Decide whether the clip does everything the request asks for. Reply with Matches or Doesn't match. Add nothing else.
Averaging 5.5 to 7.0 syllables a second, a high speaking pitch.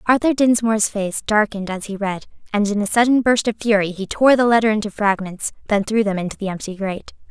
Matches